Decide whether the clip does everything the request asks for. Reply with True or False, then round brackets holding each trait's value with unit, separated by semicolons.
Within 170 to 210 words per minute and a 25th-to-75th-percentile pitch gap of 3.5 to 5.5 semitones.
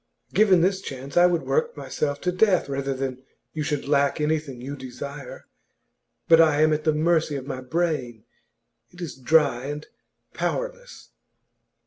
False (155 wpm; 4.0 semitones)